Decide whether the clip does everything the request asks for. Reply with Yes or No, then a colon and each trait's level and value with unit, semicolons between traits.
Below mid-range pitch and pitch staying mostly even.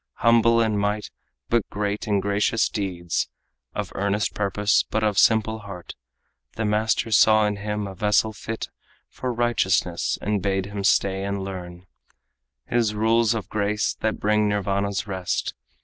Yes: low, 105 Hz; narrow, 1.7 semitones